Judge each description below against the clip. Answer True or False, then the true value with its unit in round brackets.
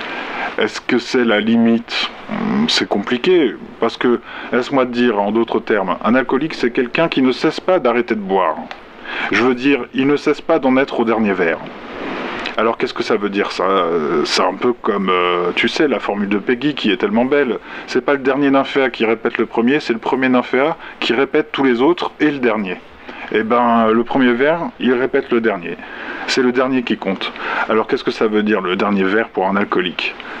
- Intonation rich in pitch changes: False (4.3 semitones)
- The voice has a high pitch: False (130 Hz)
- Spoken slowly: False (210 wpm)